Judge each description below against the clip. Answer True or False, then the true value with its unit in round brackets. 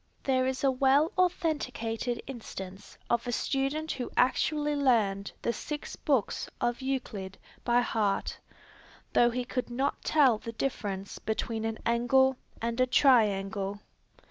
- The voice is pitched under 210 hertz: False (245 Hz)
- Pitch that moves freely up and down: False (3.4 semitones)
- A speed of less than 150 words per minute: True (135 wpm)